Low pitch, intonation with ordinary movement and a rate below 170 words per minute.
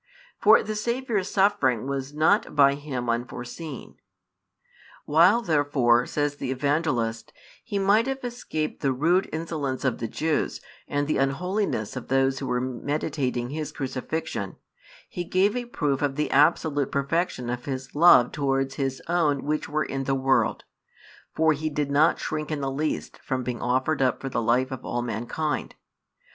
No: medium, 145 Hz; average, 3.5 semitones; average, 160 wpm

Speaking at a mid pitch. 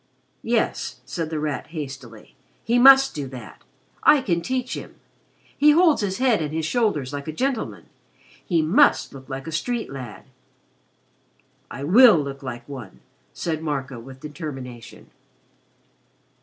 Yes: medium, 155 Hz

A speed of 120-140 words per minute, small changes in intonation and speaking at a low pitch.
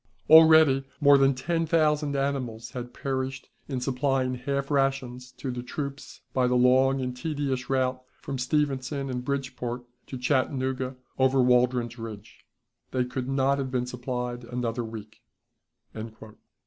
Yes: slow, 135 wpm; narrow, 1.8 semitones; low, 130 Hz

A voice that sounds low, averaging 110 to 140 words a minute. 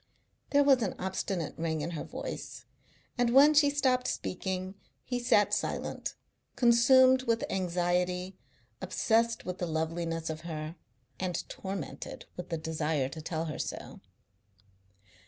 No: medium, 185 Hz; slow, 135 wpm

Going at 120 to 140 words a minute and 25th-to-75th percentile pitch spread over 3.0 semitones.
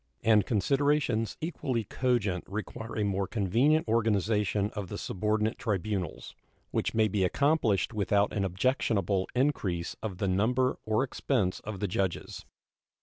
Yes: slow, 135 wpm; average, 3.6 semitones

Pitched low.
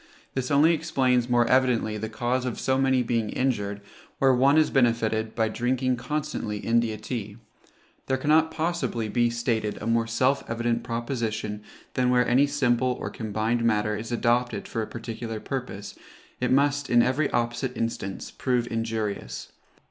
Yes: low, 120 Hz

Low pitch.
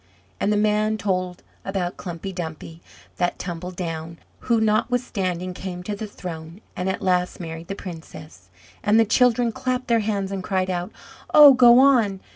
No: high, 190 Hz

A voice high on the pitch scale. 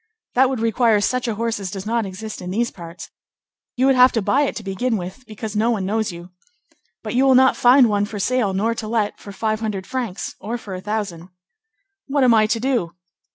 Yes: high, 220 Hz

